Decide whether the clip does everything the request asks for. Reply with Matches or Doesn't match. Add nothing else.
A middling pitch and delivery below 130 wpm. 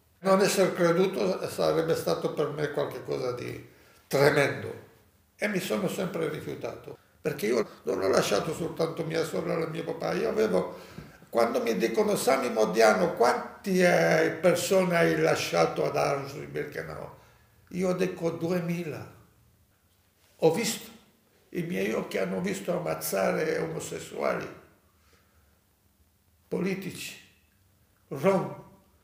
Matches